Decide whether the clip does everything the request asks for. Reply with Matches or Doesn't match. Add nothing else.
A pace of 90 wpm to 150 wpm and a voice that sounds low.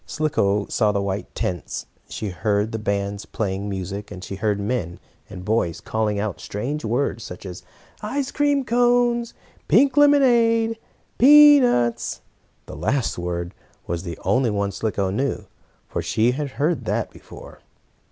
Matches